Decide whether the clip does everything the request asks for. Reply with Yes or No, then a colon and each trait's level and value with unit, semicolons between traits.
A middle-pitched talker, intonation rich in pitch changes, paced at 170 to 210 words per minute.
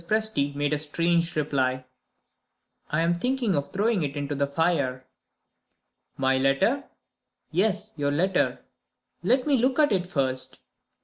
No: medium, 165 Hz; wide, 6.9 semitones; slow, 135 wpm